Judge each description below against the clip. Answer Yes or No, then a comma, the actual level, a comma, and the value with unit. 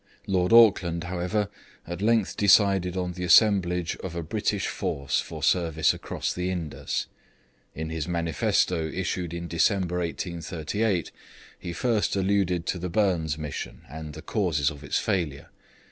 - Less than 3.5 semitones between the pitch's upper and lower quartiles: Yes, average, 2.8 semitones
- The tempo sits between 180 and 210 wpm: No, average, 145 wpm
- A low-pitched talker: Yes, very low, 90 Hz